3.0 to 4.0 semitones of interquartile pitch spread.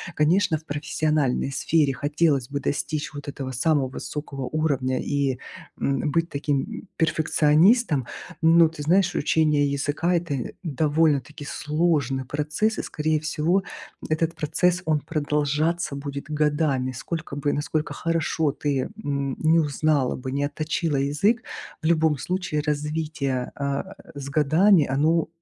No: narrow, 2.4 semitones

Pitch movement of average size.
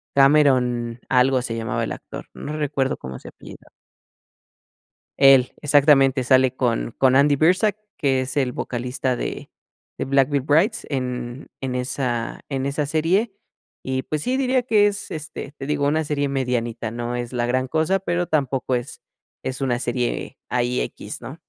Yes: average, 3.0 semitones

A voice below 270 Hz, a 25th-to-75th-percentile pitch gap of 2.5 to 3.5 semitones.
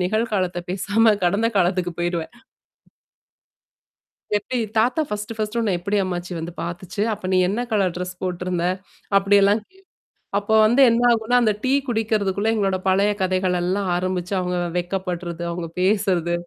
Yes: high, 190 Hz; average, 3.2 semitones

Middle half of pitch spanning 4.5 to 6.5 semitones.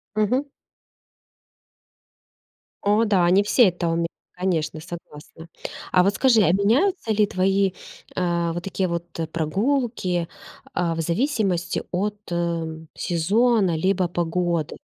No: average, 3.5 semitones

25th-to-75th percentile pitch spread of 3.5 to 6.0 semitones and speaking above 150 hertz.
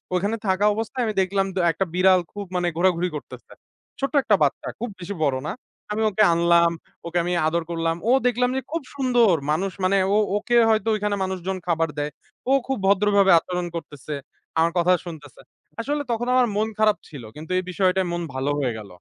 Yes: average, 4.0 semitones; medium, 185 Hz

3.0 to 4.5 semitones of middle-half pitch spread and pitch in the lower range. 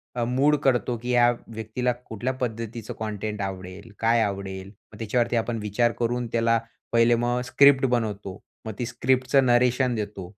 No: narrow, 2.6 semitones; low, 115 Hz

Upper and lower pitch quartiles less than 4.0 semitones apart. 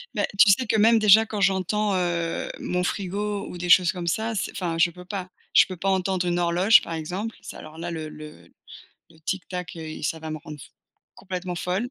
Yes: average, 2.9 semitones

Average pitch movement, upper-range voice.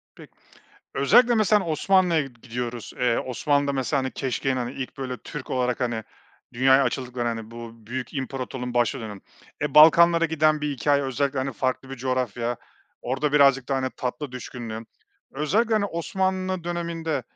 No: average, 3.8 semitones; low, 135 Hz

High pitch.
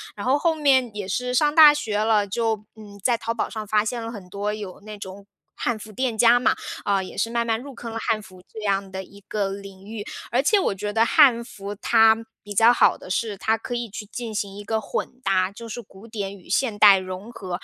Yes: high, 215 Hz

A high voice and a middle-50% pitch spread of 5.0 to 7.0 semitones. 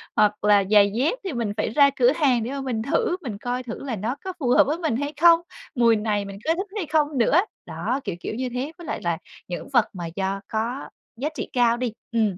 Yes: high, 245 Hz; average, 5.3 semitones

